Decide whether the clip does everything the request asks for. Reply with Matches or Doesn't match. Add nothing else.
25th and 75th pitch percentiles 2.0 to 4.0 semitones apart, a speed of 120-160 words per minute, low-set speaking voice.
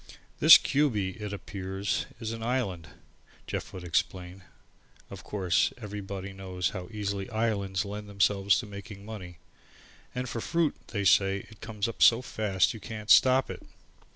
Matches